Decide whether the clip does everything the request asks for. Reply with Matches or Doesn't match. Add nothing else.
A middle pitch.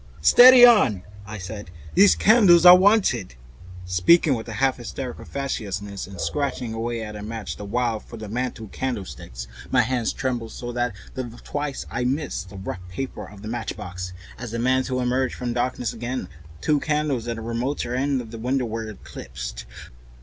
Doesn't match